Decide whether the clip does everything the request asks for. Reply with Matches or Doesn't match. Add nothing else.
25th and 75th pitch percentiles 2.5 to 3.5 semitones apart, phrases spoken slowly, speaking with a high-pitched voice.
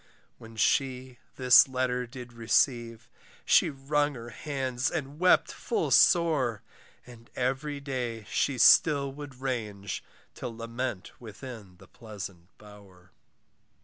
Doesn't match